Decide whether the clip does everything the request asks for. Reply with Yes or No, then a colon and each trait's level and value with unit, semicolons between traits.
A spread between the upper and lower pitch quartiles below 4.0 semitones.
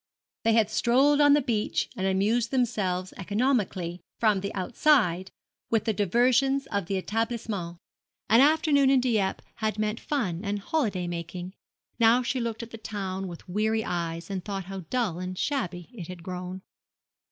No: average, 4.5 semitones